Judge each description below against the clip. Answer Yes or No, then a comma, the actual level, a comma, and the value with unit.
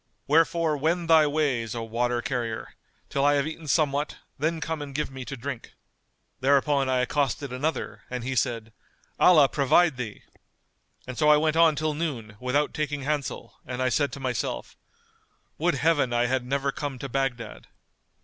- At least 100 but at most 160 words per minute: No, average, 170 wpm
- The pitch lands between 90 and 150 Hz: Yes, medium, 140 Hz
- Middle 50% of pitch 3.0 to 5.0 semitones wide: Yes, average, 3.3 semitones